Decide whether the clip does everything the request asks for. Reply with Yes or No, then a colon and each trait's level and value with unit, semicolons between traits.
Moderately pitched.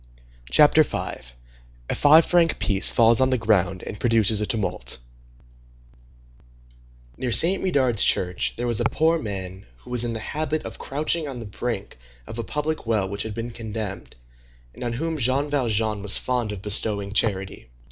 No: low, 115 Hz